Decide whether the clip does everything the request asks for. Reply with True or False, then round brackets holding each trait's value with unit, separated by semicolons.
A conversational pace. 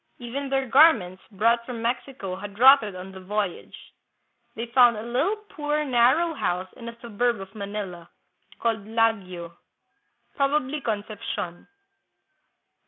False (125 wpm)